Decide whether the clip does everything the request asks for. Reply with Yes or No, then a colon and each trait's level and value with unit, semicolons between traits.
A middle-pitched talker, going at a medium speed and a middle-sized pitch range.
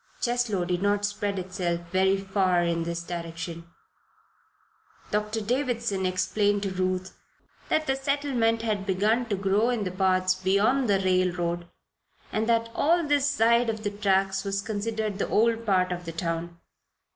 No: high, 200 Hz; average, 155 wpm; average, 3.6 semitones